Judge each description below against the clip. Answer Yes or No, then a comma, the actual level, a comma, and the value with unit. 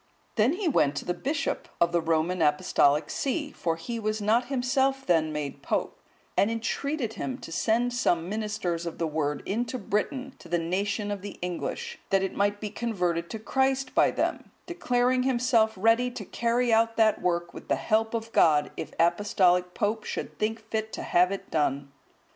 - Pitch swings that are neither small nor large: No, wide, 5.9 semitones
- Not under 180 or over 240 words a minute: Yes, average, 190 wpm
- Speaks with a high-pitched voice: Yes, high, 215 Hz